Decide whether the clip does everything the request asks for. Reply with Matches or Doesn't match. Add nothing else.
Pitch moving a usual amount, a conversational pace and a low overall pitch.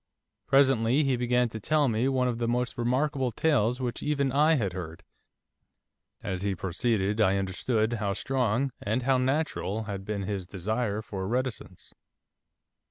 Matches